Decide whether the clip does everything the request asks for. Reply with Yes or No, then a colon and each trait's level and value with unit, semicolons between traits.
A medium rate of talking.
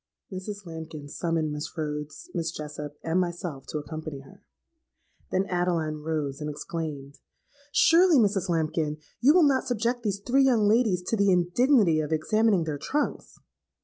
Yes: average, 150 wpm